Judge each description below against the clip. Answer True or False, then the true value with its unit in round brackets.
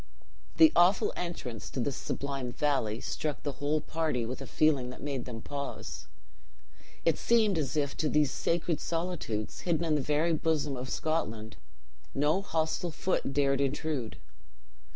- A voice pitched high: False (145 Hz)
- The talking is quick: False (150 wpm)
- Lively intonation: False (3.5 semitones)